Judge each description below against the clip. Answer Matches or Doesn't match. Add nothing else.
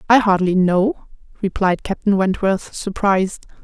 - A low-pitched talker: Doesn't match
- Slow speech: Matches